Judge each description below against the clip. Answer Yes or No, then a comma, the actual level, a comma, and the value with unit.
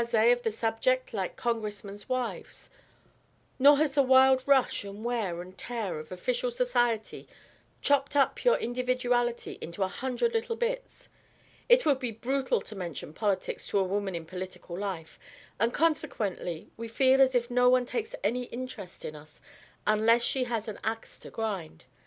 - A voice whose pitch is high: Yes, high, 235 Hz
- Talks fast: No, average, 165 wpm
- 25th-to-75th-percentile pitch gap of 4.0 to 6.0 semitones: Yes, average, 4.3 semitones